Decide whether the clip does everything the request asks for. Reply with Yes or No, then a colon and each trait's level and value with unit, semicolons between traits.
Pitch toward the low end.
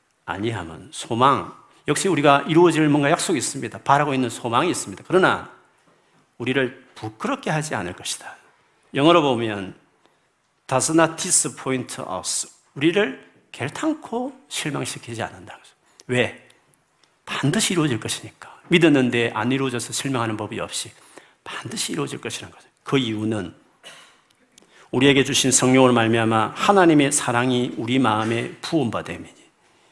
Yes: low, 130 Hz